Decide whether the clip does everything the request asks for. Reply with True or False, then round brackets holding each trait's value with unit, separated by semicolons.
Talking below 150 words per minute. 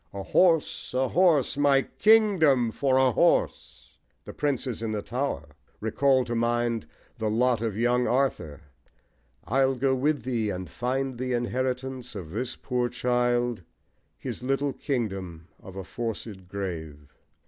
True (140 wpm)